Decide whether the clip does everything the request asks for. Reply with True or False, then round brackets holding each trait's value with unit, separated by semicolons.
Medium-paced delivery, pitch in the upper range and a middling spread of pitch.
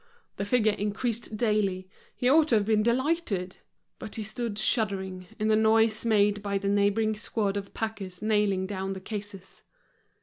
False (165 wpm; 210 Hz; 1.9 semitones)